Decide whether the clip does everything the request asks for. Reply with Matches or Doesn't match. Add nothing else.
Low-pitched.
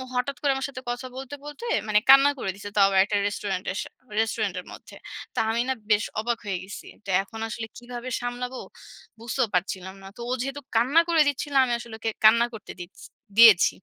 Doesn't match